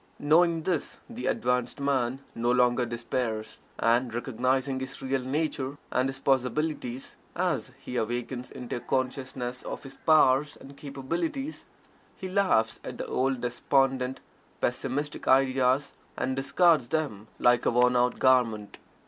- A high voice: No, low, 130 Hz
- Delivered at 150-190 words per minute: No, slow, 135 wpm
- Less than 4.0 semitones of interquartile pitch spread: Yes, narrow, 2.4 semitones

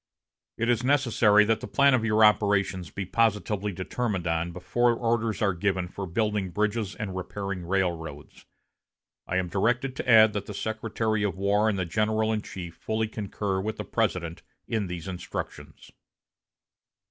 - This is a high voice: No, low, 105 Hz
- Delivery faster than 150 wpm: Yes, average, 160 wpm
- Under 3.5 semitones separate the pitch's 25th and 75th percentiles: Yes, average, 2.9 semitones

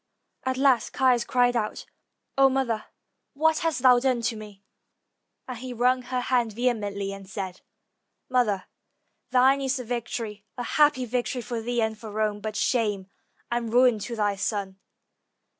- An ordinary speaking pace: Yes, average, 160 wpm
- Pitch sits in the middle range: No, high, 240 Hz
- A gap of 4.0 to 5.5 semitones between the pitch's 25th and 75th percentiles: No, average, 3.1 semitones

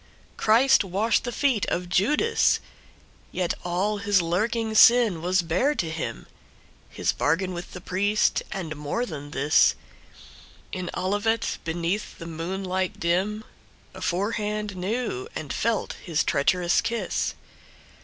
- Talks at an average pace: No, slow, 110 wpm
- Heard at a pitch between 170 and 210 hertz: Yes, high, 190 Hz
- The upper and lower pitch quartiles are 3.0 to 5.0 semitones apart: Yes, average, 3.9 semitones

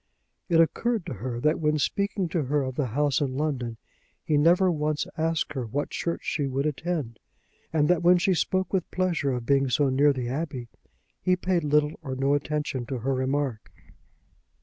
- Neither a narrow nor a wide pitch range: Yes, average, 3.9 semitones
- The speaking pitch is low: No, medium, 150 Hz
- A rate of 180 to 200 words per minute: Yes, average, 190 wpm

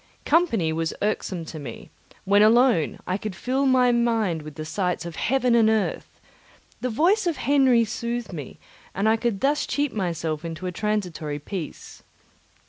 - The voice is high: Yes, high, 215 Hz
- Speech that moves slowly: No, average, 165 wpm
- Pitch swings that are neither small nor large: No, wide, 6.6 semitones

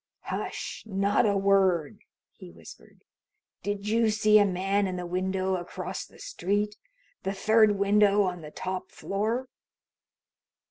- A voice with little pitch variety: Yes, narrow, 2.1 semitones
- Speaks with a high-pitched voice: Yes, high, 195 Hz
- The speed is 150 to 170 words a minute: No, slow, 135 wpm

